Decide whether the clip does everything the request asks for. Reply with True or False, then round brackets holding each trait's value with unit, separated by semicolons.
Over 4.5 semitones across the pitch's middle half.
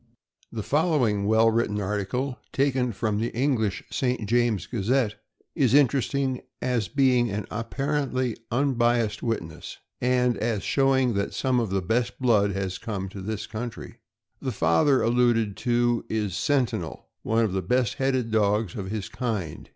False (3.5 semitones)